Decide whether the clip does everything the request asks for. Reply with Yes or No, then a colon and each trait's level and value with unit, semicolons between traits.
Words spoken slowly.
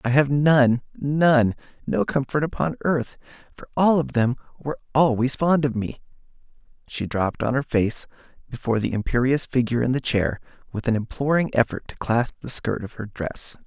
No: average, 175 wpm